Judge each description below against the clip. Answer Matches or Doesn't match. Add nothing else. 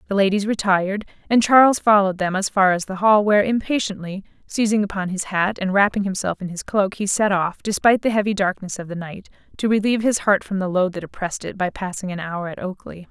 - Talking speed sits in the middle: Doesn't match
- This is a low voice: Doesn't match